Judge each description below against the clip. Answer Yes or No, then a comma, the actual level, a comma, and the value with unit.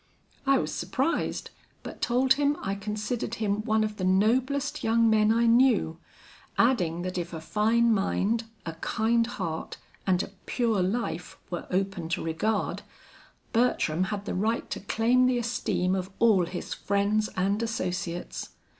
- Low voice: No, high, 215 Hz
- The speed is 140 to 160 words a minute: Yes, average, 155 wpm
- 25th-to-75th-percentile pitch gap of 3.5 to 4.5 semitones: Yes, average, 4.1 semitones